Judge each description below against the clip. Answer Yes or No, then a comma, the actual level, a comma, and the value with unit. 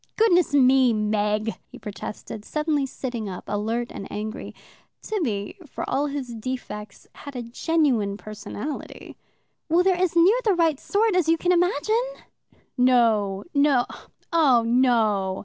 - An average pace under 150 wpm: Yes, average, 140 wpm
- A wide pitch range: Yes, wide, 7.2 semitones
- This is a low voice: No, very high, 255 Hz